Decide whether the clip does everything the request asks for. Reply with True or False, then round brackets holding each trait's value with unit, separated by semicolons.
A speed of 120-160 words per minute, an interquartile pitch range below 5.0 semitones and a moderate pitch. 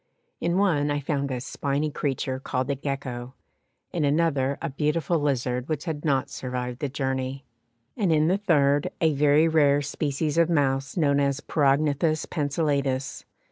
True (155 wpm; 2.4 semitones; 145 Hz)